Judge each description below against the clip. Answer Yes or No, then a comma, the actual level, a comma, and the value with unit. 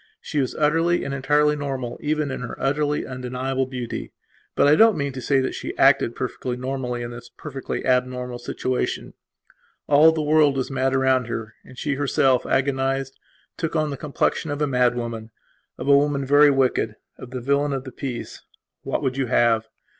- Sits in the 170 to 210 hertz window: No, low, 135 Hz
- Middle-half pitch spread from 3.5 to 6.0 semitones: No, narrow, 2.4 semitones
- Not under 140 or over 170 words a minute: No, average, 185 wpm